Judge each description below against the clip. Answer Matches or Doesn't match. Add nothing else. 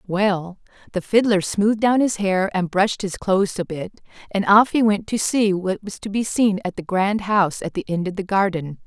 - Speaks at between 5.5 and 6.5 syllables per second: Doesn't match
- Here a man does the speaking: Doesn't match